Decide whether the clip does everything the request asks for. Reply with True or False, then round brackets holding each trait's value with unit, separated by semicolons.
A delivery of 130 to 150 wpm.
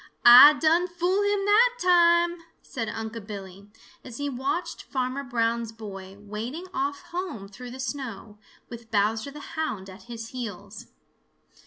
True (145 wpm)